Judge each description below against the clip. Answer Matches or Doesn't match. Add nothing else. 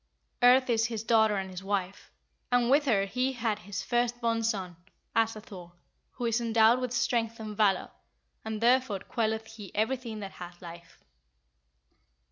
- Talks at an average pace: Matches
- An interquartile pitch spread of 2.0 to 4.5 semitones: Matches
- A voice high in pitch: Matches